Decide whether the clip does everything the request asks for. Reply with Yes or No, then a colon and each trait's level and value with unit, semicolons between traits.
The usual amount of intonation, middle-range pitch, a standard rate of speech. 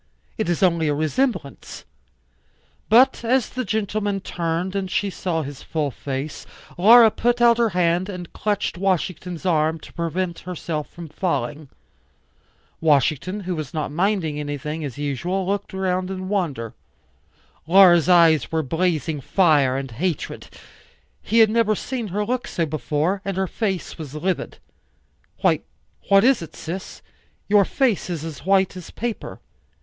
Yes: average, 4.2 semitones; medium, 180 Hz; average, 150 wpm